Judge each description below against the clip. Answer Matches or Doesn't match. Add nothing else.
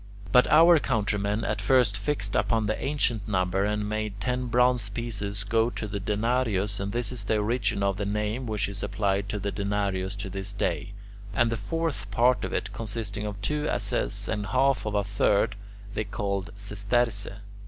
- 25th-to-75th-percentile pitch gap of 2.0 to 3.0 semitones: Matches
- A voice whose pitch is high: Doesn't match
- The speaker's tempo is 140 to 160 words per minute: Doesn't match